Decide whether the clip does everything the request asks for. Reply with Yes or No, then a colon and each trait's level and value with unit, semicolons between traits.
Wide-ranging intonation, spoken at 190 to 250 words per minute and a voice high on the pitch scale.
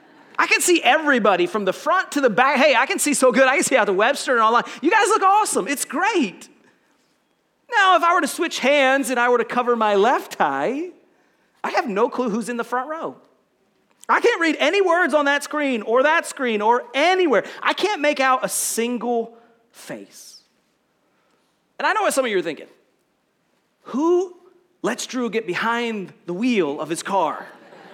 Yes: wide, 6.4 semitones; average, 200 wpm; very high, 270 Hz